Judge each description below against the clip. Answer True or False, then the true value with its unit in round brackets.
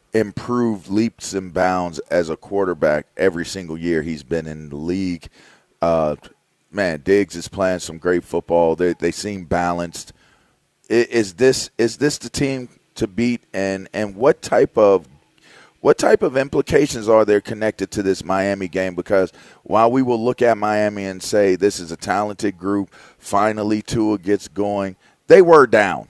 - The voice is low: True (100 Hz)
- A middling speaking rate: True (170 wpm)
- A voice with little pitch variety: False (4.0 semitones)